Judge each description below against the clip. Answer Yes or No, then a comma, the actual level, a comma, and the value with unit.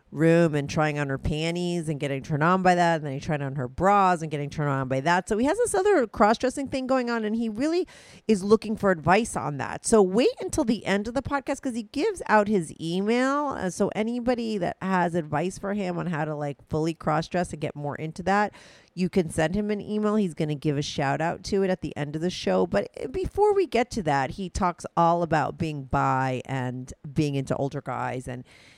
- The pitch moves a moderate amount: No, wide, 6.4 semitones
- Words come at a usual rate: No, fast, 240 wpm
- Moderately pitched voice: Yes, medium, 175 Hz